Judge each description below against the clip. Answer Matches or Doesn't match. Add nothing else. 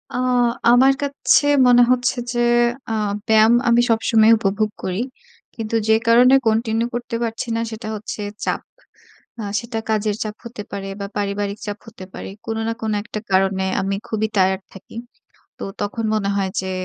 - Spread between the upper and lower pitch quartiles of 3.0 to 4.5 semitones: Doesn't match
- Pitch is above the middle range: Matches